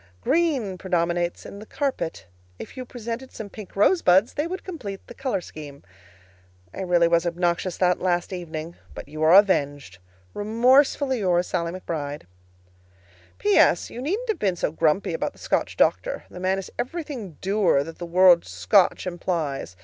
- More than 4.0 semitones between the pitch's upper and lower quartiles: Yes, wide, 5.6 semitones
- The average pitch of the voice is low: No, medium, 185 Hz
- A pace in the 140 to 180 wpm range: Yes, average, 160 wpm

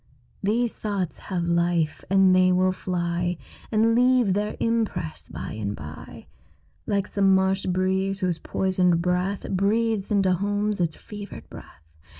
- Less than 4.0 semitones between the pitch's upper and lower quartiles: Yes, narrow, 2.6 semitones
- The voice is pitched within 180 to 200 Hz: Yes, high, 190 Hz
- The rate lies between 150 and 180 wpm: No, average, 140 wpm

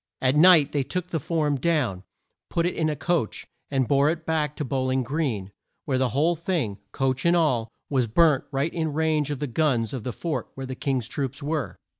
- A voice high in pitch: No, medium, 145 Hz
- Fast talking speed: Yes, fast, 215 wpm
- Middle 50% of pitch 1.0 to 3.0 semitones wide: No, average, 3.6 semitones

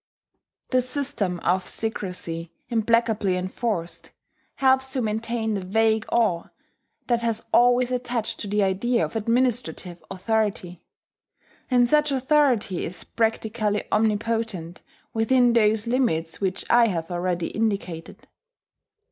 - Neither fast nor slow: No, slow, 115 wpm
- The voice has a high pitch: Yes, high, 220 Hz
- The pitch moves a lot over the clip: No, average, 4.3 semitones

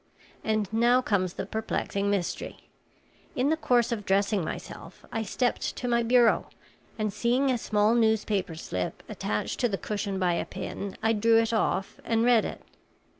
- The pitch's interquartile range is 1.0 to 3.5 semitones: Yes, average, 2.9 semitones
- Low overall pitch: No, high, 220 Hz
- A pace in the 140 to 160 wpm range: No, average, 170 wpm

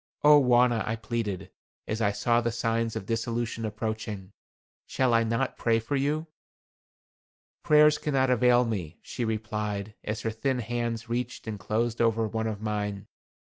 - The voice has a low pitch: Yes, low, 115 Hz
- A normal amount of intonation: No, narrow, 1.9 semitones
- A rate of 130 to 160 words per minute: Yes, average, 155 wpm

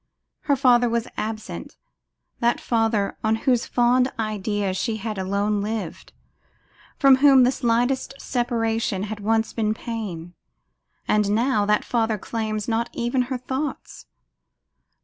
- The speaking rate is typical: No, slow, 130 wpm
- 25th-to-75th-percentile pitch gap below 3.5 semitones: Yes, narrow, 2.5 semitones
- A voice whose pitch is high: Yes, high, 225 Hz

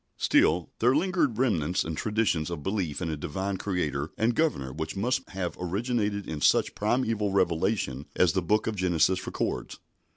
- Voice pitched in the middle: No, very low, 95 Hz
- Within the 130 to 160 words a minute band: No, average, 170 wpm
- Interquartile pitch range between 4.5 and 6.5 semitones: Yes, average, 5.3 semitones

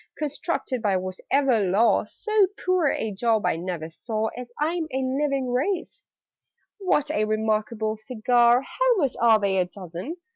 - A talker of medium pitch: No, high, 235 Hz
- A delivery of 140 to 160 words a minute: Yes, average, 155 wpm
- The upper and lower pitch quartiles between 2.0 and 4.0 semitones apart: No, average, 5.2 semitones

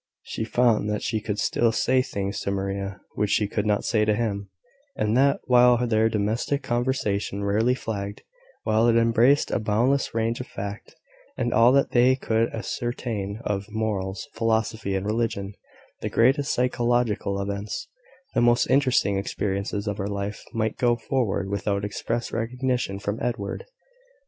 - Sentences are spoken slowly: No, average, 155 wpm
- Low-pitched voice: Yes, low, 110 Hz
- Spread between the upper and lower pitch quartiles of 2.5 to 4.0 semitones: Yes, average, 3.1 semitones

